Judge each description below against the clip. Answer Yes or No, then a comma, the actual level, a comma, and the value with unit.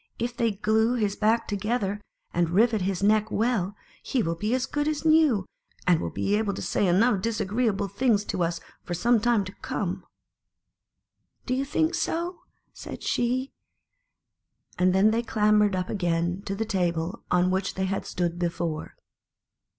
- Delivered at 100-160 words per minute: No, average, 175 wpm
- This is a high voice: Yes, high, 210 Hz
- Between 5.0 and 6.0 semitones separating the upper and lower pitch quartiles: No, average, 4.2 semitones